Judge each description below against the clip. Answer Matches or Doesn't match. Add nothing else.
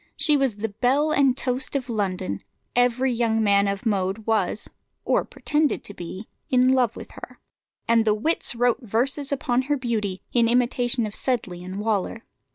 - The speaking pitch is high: Matches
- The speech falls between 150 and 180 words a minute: Matches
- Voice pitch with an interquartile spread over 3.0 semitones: Matches